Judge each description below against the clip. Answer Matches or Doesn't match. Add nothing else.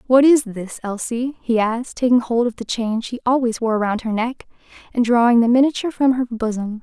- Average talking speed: Doesn't match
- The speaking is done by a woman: Matches